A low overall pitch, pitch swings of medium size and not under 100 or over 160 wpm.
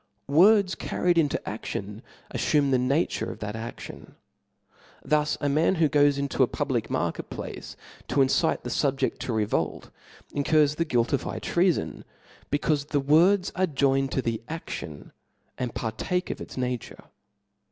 No: medium, 145 Hz; average, 4.1 semitones; average, 150 wpm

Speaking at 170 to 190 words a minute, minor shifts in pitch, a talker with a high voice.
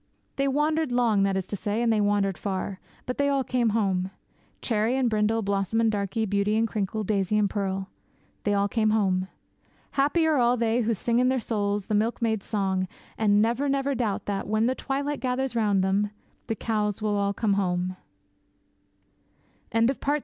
No: average, 180 wpm; average, 3.2 semitones; high, 215 Hz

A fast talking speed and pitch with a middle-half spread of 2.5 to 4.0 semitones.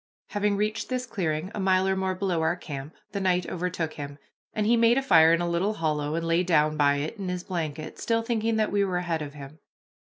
No: fast, 240 wpm; average, 4.4 semitones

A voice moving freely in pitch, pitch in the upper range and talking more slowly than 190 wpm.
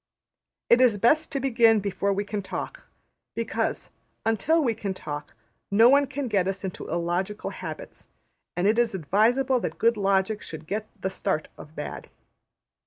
No: average, 3.8 semitones; high, 205 Hz; average, 165 wpm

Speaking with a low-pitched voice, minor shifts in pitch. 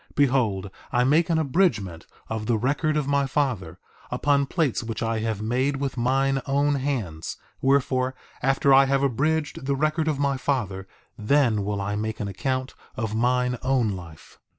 No: low, 130 Hz; average, 4.3 semitones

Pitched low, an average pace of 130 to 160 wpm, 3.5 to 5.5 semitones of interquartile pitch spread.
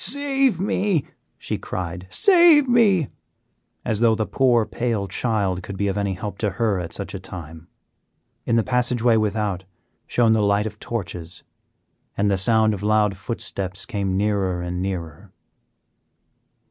Yes: low, 105 Hz; average, 150 wpm; average, 4.0 semitones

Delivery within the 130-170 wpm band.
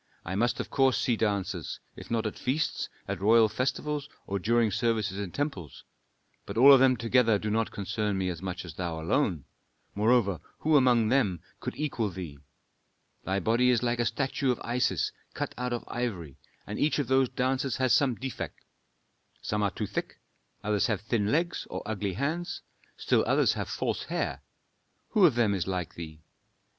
No: average, 180 wpm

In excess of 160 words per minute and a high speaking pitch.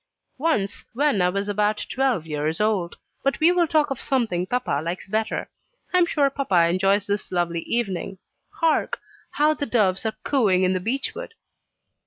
Yes: average, 175 wpm; high, 215 Hz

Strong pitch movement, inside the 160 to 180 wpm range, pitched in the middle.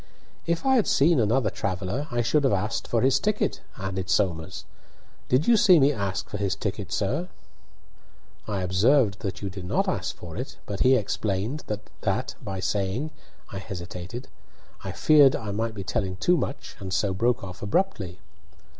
No: wide, 5.8 semitones; average, 175 wpm; low, 105 Hz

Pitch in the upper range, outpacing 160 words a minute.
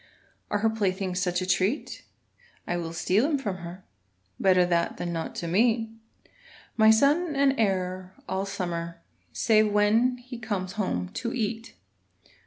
No: high, 195 Hz; average, 150 wpm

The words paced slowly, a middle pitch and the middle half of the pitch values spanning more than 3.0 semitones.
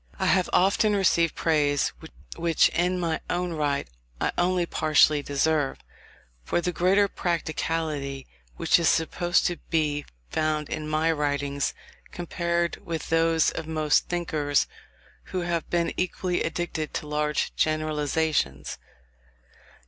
No: slow, 125 wpm; medium, 160 Hz; narrow, 2.4 semitones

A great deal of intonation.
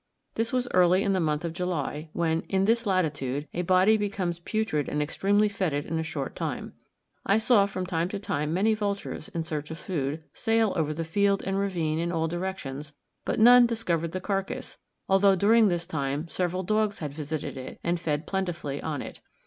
No: average, 4.2 semitones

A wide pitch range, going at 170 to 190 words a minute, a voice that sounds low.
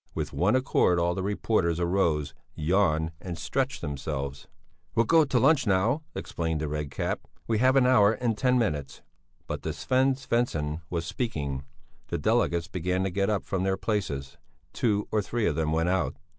Yes: wide, 6.3 semitones; average, 175 wpm; very low, 95 Hz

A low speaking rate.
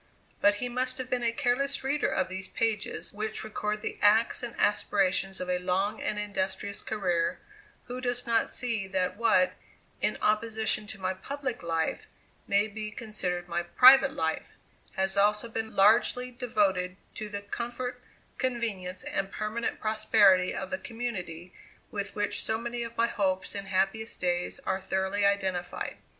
No: average, 160 wpm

